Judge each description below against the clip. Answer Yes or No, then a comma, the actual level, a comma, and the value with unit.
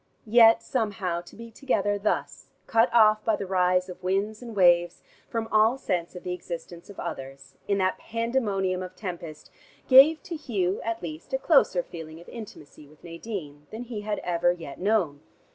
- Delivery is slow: No, average, 180 wpm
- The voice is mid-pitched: No, high, 195 Hz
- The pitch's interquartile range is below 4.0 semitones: No, average, 4.5 semitones